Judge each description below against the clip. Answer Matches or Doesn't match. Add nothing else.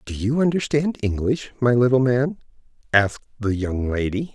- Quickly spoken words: Doesn't match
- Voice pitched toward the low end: Matches